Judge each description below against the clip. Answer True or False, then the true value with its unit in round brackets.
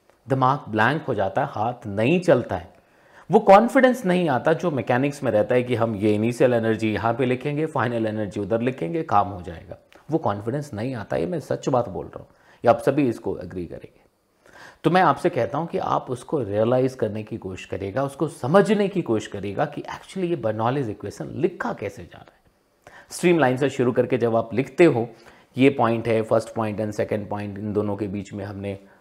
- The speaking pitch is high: False (125 Hz)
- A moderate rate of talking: False (210 wpm)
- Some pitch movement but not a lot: False (5.7 semitones)